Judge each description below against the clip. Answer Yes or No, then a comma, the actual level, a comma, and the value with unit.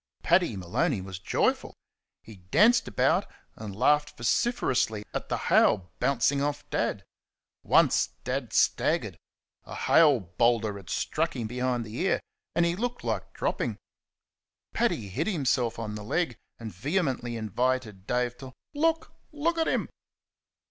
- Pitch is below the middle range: Yes, low, 125 Hz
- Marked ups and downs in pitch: Yes, wide, 7.4 semitones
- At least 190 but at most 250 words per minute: No, average, 140 wpm